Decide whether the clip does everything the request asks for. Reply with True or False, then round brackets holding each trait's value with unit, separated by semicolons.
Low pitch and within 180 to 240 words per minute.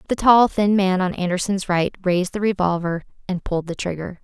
False (190 Hz; 200 wpm)